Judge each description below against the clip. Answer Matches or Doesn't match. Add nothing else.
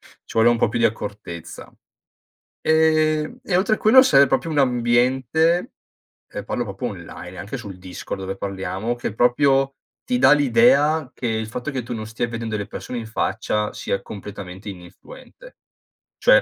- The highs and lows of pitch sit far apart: Matches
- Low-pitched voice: Matches